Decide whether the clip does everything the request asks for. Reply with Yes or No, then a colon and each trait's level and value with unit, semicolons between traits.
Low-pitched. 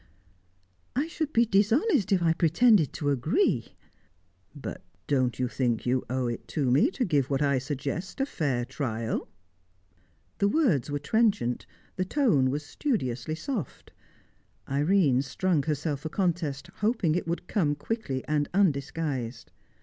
No: medium, 155 Hz